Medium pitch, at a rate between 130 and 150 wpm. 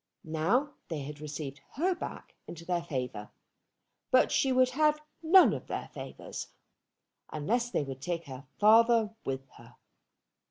Yes: medium, 175 Hz; average, 145 wpm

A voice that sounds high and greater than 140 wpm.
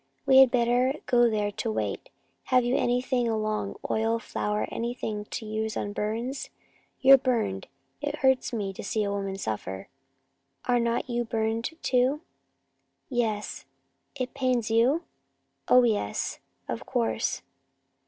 No: high, 235 Hz; slow, 135 wpm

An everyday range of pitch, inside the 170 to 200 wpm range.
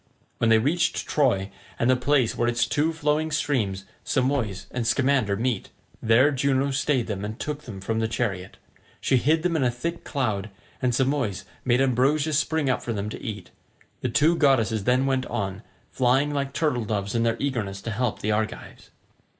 Yes: average, 4.2 semitones; average, 185 wpm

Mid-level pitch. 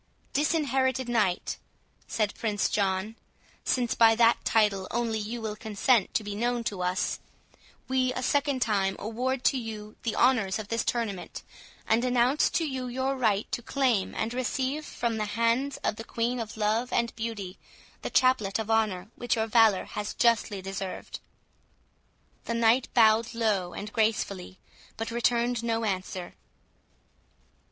No: high, 225 Hz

